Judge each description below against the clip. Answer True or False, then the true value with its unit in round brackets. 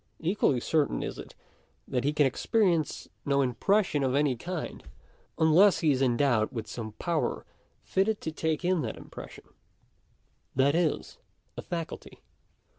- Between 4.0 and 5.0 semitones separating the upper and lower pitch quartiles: True (4.7 semitones)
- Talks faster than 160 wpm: False (145 wpm)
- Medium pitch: True (150 Hz)